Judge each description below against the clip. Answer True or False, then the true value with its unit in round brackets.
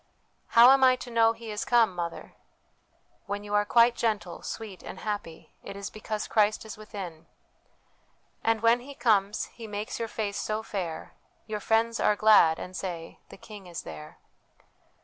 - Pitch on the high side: True (210 Hz)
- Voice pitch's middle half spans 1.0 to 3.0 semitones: True (2.6 semitones)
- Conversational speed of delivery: True (190 wpm)